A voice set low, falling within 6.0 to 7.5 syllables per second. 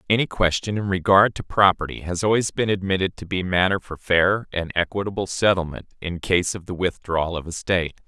No: very low, 90 Hz; 5.6 syllables/s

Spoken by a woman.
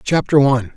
No: male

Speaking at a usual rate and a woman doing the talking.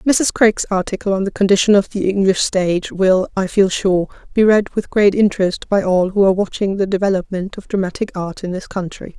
No: fast, 210 wpm; female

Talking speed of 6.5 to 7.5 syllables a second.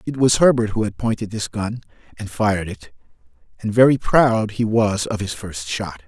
No: 5.0 syllables/s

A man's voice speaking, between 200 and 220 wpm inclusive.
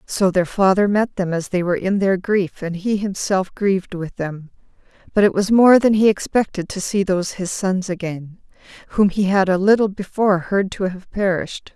No: female; fast, 205 wpm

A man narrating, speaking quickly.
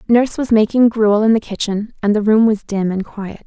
No: female; fast, 245 wpm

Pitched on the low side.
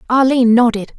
No: high, 240 Hz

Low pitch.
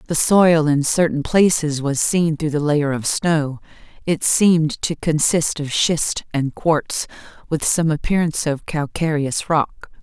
No: medium, 155 Hz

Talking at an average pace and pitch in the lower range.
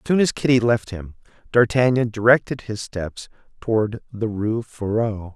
Yes: average, 145 wpm; low, 115 Hz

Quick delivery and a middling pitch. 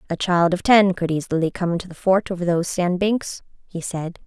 Yes: fast, 225 wpm; medium, 180 Hz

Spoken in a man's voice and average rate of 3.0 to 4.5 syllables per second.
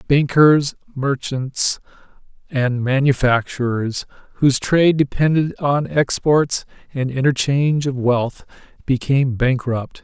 Yes: male; 4.0 syllables/s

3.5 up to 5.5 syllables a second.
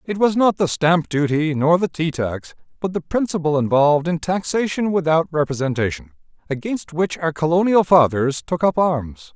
Yes: 4.9 syllables/s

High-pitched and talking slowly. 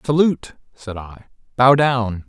No: low, 120 Hz; slow, 130 wpm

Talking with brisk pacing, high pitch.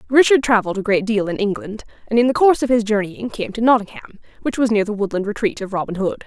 Yes: fast, 250 wpm; high, 215 Hz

